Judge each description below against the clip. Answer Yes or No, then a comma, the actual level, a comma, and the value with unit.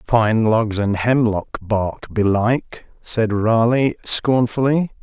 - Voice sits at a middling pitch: No, low, 115 Hz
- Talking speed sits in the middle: No, slow, 110 wpm